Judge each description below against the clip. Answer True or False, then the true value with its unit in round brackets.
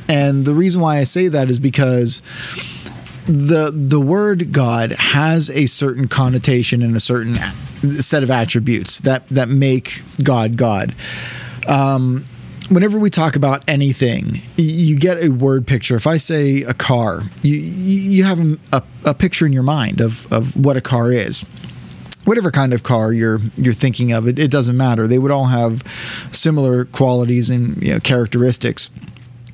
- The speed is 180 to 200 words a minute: False (165 wpm)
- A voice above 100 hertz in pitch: True (135 Hz)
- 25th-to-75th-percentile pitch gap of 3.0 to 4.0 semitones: True (3.7 semitones)